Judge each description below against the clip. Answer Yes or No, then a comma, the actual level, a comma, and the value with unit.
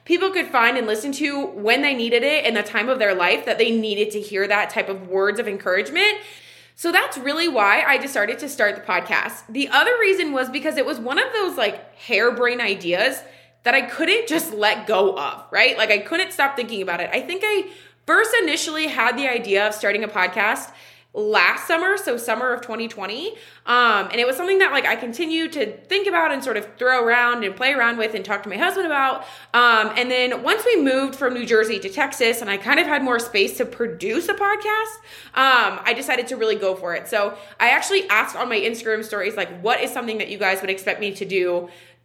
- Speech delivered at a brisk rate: Yes, fast, 230 wpm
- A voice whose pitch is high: Yes, high, 240 Hz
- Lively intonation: Yes, wide, 7.1 semitones